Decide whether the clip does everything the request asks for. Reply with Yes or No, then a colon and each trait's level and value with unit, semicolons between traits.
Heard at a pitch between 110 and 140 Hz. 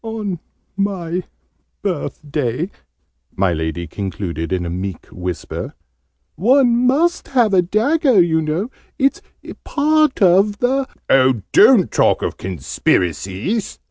No: medium, 180 Hz